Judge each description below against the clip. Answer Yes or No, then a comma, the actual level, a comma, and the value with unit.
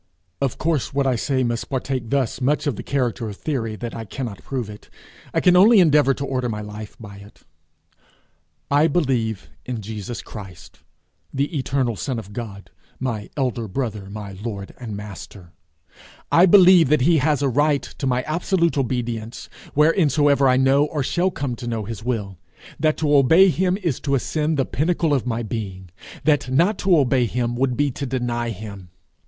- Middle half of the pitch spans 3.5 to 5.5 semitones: Yes, average, 4.8 semitones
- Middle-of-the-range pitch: No, low, 130 Hz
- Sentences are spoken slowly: No, average, 180 wpm